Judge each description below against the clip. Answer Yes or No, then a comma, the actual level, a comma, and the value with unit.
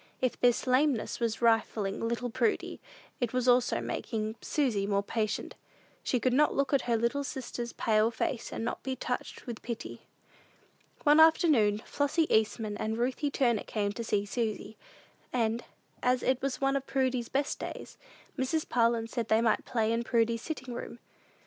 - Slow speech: No, average, 170 wpm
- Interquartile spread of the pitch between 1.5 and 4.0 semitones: Yes, average, 2.8 semitones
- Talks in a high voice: Yes, high, 235 Hz